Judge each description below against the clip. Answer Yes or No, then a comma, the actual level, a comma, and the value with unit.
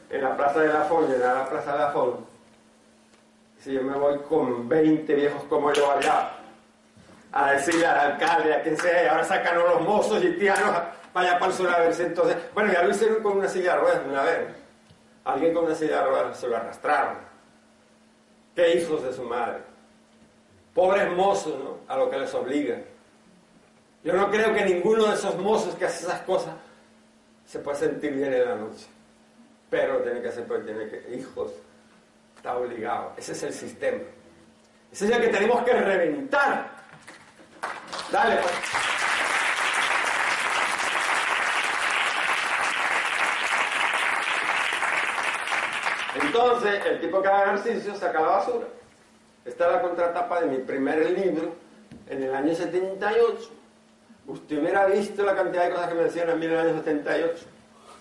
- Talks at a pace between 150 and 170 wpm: Yes, average, 160 wpm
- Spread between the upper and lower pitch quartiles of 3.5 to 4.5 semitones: No, wide, 5.6 semitones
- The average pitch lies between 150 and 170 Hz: No, medium, 180 Hz